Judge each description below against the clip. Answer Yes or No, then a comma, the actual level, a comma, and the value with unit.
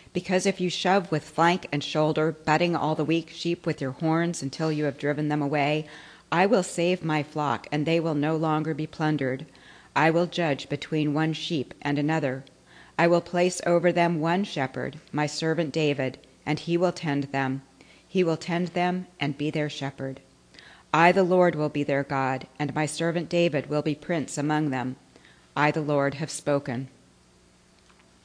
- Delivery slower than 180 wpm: No, average, 185 wpm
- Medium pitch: Yes, medium, 155 Hz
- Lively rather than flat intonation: No, average, 3.0 semitones